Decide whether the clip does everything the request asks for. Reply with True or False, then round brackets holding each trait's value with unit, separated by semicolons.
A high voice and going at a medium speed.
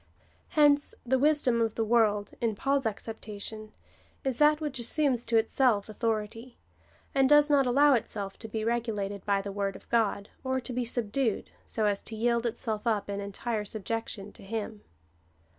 True (225 Hz; 175 wpm)